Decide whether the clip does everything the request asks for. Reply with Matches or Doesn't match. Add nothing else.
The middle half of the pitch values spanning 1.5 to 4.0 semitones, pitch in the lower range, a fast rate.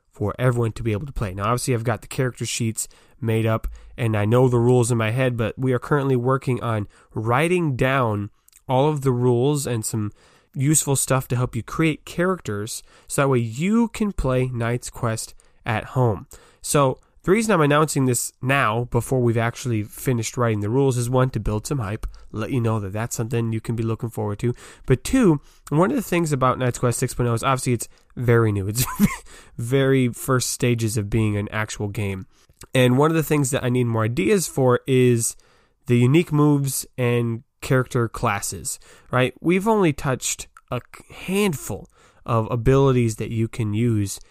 Doesn't match